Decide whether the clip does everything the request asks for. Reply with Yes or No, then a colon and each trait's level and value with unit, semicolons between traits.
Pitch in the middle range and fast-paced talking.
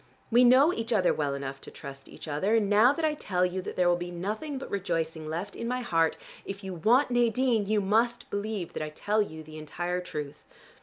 No: high, 195 Hz; fast, 225 wpm